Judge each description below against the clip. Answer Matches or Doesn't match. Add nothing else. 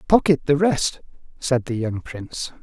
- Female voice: Doesn't match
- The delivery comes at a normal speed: Matches